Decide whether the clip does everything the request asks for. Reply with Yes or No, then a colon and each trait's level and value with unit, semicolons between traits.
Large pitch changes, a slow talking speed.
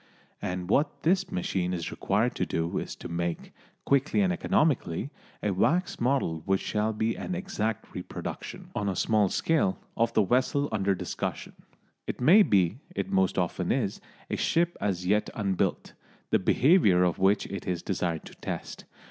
No: wide, 7.4 semitones; average, 165 wpm